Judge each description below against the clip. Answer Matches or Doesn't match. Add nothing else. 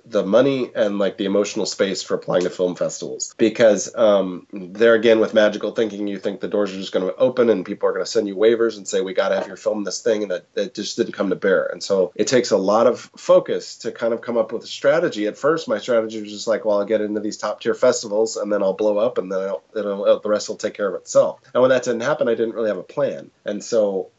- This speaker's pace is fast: Matches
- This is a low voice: Matches